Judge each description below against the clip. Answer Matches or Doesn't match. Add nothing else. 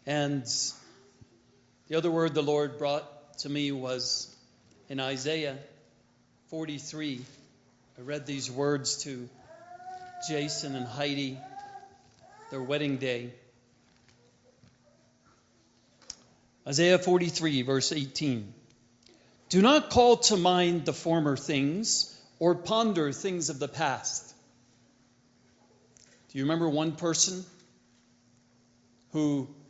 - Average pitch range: Matches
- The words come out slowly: Matches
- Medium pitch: Matches